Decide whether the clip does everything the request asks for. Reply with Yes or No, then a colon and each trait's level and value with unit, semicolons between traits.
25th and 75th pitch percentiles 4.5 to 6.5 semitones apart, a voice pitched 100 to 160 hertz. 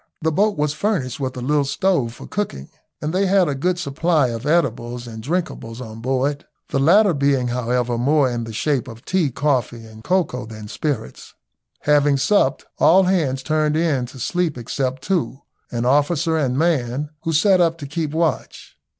Yes: average, 4.9 semitones; medium, 140 Hz